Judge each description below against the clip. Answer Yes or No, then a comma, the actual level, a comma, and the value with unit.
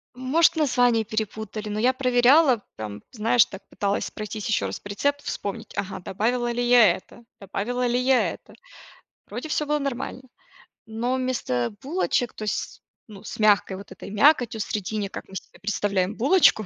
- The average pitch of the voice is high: Yes, high, 225 Hz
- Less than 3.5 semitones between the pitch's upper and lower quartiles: No, average, 3.8 semitones